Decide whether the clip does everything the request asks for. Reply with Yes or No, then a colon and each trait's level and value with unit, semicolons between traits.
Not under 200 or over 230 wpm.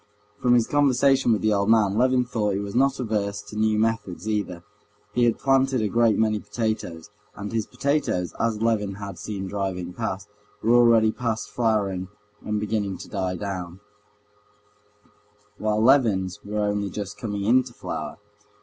No: average, 160 wpm